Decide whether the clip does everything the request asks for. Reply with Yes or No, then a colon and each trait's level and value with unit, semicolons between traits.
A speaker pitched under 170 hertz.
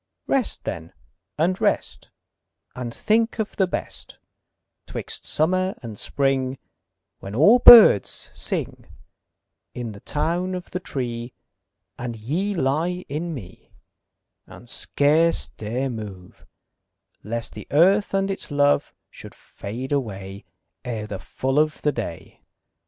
Yes: medium, 140 Hz